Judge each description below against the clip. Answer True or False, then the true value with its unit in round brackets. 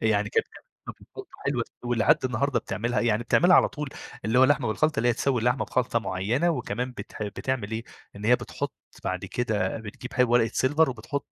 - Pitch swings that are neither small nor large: True (3.0 semitones)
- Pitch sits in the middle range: False (120 Hz)